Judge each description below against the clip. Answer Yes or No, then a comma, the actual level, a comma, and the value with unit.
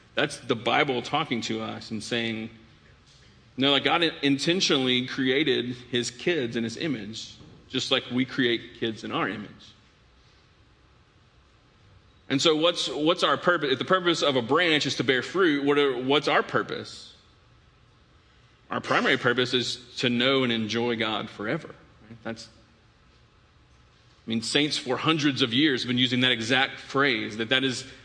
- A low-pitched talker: Yes, low, 125 Hz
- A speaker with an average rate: Yes, average, 165 wpm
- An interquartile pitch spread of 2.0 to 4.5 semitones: Yes, average, 3.6 semitones